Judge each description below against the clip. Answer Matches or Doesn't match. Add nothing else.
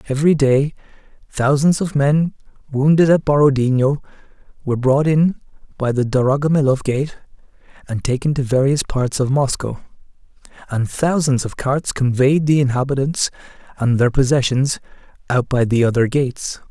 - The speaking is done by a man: Matches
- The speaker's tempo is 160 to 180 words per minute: Doesn't match